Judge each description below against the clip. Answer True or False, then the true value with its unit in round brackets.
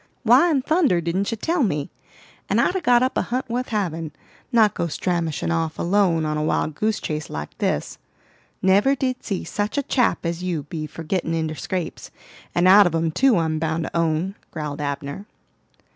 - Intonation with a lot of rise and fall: True (5.7 semitones)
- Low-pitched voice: False (175 Hz)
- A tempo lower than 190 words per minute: False (195 wpm)